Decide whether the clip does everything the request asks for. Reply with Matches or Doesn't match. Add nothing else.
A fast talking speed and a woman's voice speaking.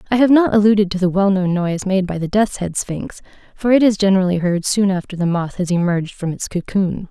Matches